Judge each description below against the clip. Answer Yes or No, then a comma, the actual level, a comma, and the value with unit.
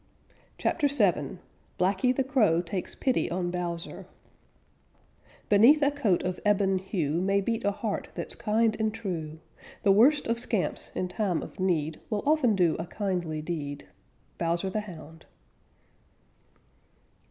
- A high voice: Yes, high, 195 Hz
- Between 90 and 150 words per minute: Yes, average, 140 wpm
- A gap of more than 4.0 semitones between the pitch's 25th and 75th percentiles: Yes, average, 4.4 semitones